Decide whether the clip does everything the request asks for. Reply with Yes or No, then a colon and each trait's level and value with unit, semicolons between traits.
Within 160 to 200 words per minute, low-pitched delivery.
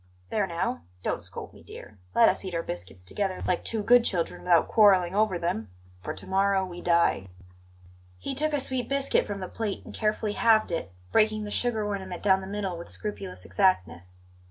No: average, 195 wpm; high, 190 Hz